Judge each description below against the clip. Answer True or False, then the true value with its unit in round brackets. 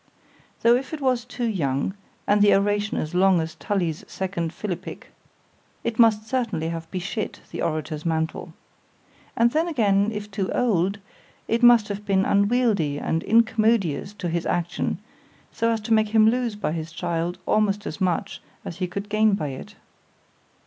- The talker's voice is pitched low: False (200 Hz)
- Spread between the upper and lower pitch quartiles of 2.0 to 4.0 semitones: False (4.7 semitones)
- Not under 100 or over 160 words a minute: True (155 wpm)